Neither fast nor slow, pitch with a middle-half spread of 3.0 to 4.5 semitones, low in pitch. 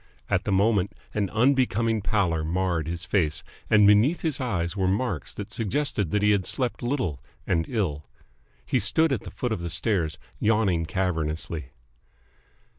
No: average, 160 wpm; average, 4.9 semitones; low, 100 Hz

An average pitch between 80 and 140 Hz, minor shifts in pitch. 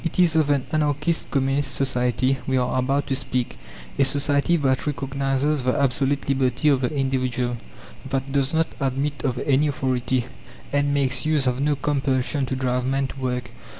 Yes: low, 135 Hz; narrow, 1.8 semitones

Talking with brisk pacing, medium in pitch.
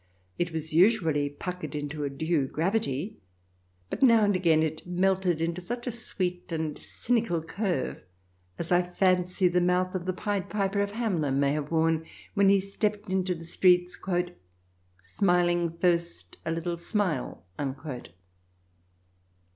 No: average, 140 wpm; medium, 175 Hz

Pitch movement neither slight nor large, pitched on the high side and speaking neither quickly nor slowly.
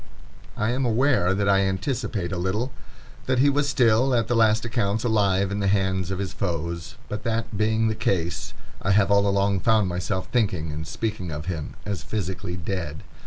No: average, 3.3 semitones; low, 100 Hz; average, 190 wpm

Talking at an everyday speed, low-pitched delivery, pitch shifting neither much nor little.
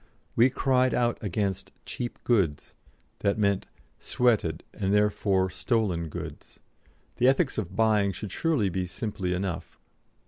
No: slow, 130 wpm; low, 105 Hz; average, 4.0 semitones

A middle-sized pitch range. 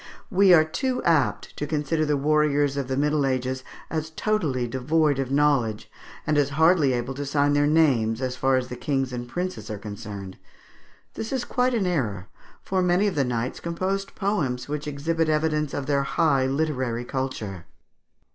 Yes: average, 3.8 semitones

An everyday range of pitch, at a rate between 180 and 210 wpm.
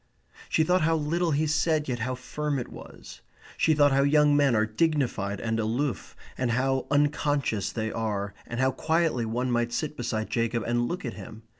Yes: average, 4.4 semitones; average, 190 wpm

